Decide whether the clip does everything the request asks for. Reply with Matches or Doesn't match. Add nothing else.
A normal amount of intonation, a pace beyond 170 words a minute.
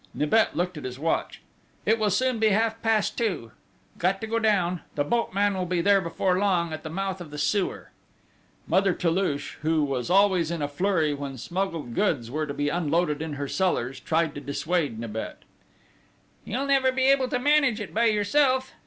Doesn't match